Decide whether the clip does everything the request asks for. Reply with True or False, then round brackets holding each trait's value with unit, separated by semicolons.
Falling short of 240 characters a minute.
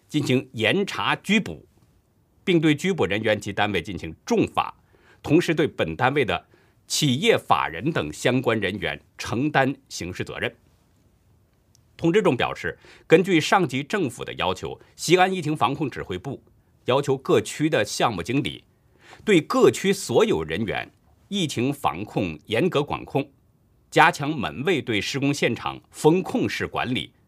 True (225 characters per minute)